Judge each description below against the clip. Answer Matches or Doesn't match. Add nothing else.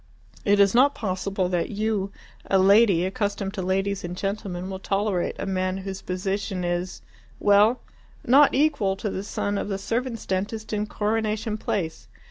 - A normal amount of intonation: Doesn't match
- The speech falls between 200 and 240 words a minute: Doesn't match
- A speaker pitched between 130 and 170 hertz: Doesn't match